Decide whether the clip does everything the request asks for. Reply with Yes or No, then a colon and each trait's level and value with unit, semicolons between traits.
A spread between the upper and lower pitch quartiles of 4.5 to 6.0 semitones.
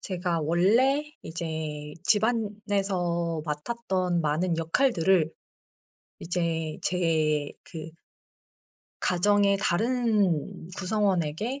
No: average, 4.1 semitones